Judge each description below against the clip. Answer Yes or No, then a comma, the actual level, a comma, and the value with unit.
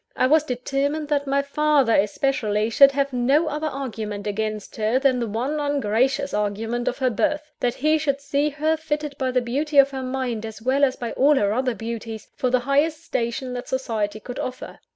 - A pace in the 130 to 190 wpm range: No, average, 200 wpm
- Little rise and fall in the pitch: No, average, 3.7 semitones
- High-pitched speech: Yes, very high, 260 Hz